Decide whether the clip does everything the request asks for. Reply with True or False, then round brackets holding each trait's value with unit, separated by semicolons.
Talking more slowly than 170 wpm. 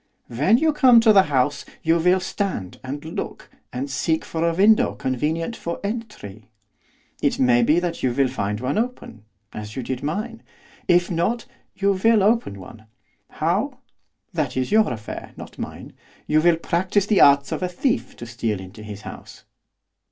False (175 wpm)